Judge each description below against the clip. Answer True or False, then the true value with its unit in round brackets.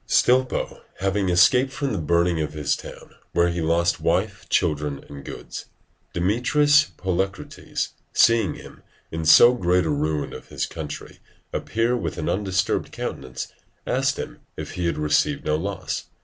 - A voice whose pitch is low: True (90 Hz)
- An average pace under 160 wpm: True (150 wpm)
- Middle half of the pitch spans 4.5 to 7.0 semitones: True (4.8 semitones)